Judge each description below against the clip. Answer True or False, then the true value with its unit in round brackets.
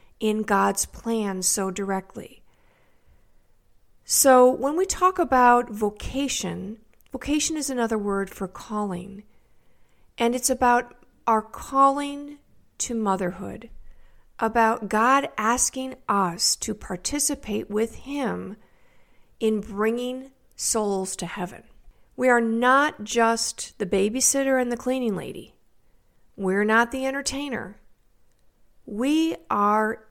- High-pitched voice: True (230 Hz)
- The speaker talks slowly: True (105 wpm)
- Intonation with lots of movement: False (4.2 semitones)